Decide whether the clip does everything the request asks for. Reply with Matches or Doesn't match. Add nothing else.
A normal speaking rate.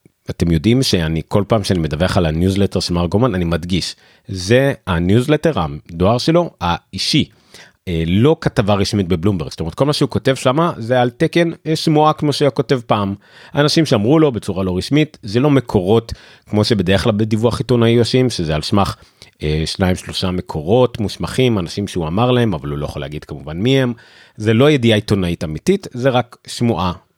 Doesn't match